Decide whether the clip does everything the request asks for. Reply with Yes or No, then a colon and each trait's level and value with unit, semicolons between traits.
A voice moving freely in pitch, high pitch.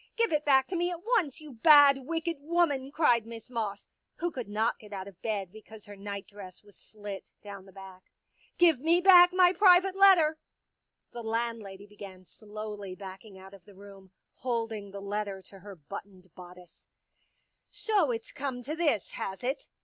Yes: wide, 7.4 semitones; high, 220 Hz